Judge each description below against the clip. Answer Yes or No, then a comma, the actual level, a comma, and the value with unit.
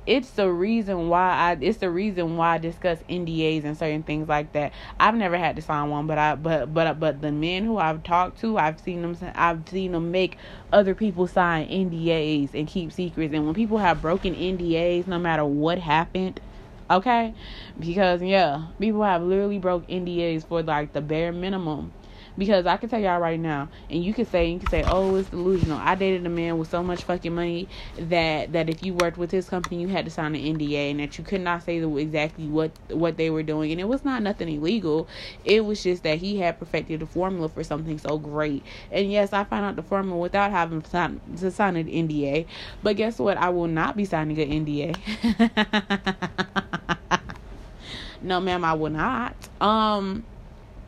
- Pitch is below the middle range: No, medium, 170 Hz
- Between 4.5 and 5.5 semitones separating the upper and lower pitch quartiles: No, average, 3.1 semitones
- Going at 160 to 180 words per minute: No, fast, 205 wpm